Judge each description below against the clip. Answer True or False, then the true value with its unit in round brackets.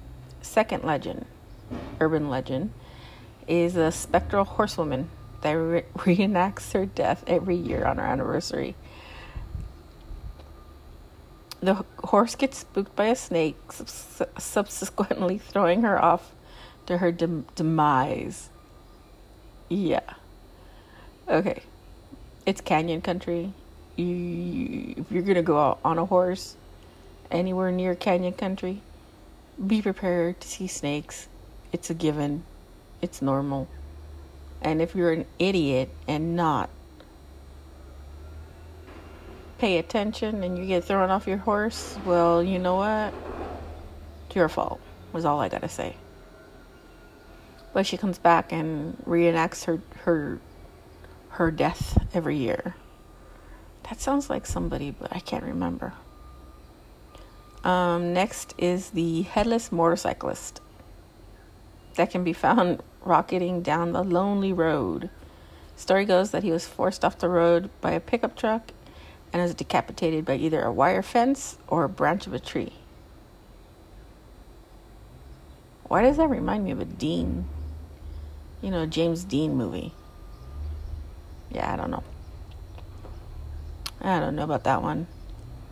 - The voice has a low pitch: False (160 Hz)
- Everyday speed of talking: False (125 wpm)